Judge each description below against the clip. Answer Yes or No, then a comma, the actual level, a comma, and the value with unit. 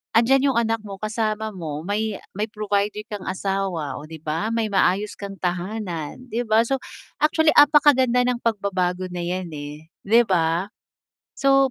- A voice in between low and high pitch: No, high, 205 Hz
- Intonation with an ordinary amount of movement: Yes, average, 4.3 semitones